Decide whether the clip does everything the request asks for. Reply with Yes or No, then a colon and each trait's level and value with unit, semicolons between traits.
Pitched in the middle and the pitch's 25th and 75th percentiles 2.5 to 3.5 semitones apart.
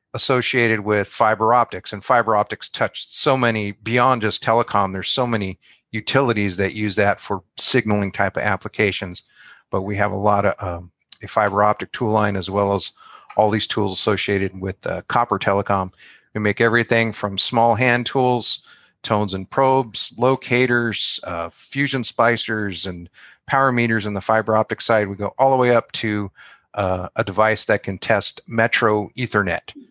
No: low, 105 Hz; average, 2.8 semitones